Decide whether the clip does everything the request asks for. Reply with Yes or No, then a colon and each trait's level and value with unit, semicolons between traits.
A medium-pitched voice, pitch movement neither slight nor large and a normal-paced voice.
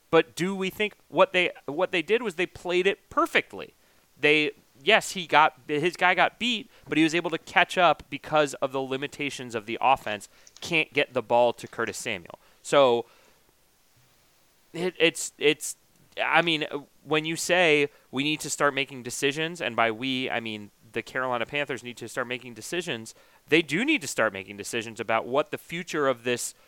No: medium, 145 Hz; wide, 5.7 semitones; average, 190 wpm